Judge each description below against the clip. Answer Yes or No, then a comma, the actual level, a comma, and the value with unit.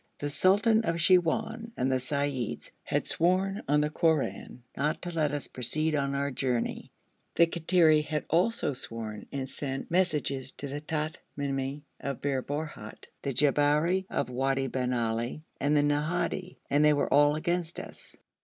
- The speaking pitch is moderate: Yes, medium, 145 Hz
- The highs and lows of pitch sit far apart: No, average, 3.5 semitones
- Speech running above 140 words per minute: Yes, average, 160 wpm